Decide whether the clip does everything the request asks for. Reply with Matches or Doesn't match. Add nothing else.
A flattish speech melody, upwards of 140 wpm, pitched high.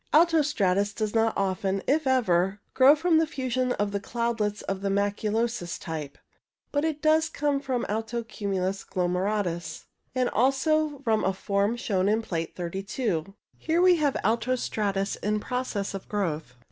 Doesn't match